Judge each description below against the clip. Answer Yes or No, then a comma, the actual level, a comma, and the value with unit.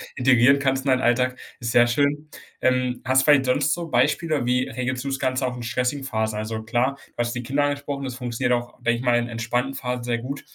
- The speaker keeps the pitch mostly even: Yes, narrow, 2.2 semitones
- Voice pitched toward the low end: Yes, low, 125 Hz